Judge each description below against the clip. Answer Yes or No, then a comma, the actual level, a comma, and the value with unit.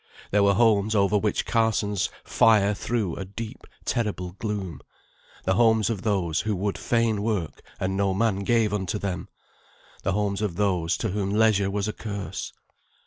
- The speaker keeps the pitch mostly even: Yes, narrow, 2.1 semitones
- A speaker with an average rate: Yes, average, 165 wpm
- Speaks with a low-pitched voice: Yes, low, 100 Hz